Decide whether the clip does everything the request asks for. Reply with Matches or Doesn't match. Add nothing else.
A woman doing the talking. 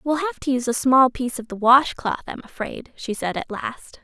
Matches